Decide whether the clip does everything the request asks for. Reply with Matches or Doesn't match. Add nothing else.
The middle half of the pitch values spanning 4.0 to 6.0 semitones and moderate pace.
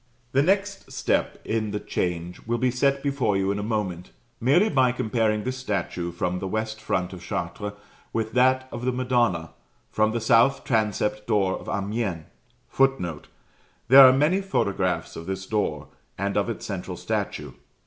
Matches